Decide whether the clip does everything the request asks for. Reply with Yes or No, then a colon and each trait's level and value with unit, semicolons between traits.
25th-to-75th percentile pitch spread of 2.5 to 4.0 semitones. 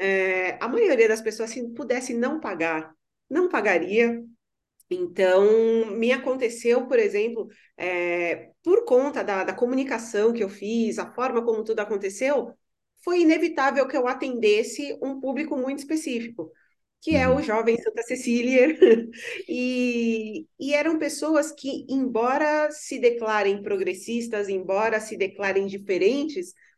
No: average, 5.3 semitones